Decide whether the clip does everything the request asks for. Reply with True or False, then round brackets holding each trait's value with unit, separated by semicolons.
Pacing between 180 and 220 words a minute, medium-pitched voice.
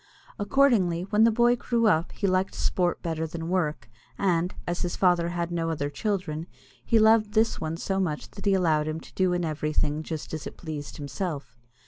True (195 wpm; 175 Hz)